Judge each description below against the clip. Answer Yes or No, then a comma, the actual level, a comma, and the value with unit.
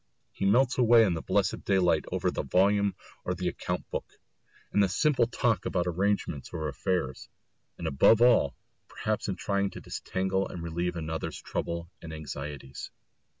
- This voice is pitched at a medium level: No, very low, 90 Hz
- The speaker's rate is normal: Yes, average, 160 wpm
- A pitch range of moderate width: Yes, average, 4.0 semitones